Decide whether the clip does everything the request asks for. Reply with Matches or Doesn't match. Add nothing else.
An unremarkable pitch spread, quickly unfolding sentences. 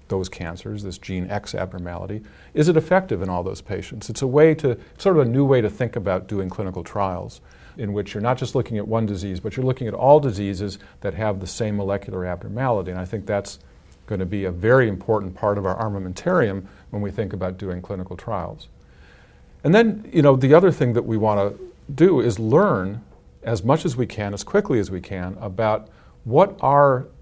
Matches